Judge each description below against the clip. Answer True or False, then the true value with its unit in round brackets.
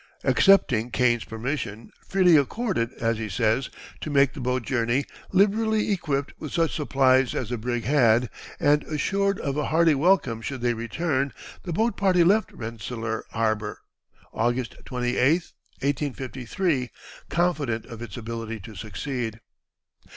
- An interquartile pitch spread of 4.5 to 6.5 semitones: True (5.2 semitones)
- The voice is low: True (130 Hz)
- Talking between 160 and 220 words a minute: False (135 wpm)